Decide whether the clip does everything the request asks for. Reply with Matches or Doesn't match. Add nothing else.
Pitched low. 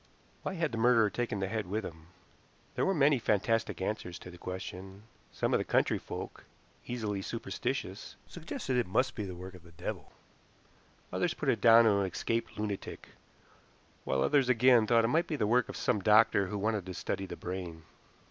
Matches